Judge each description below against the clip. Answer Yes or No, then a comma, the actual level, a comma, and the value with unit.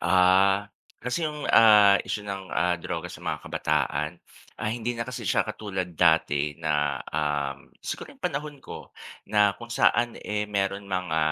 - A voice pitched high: No, low, 100 Hz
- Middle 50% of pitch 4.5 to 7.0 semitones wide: Yes, average, 5.0 semitones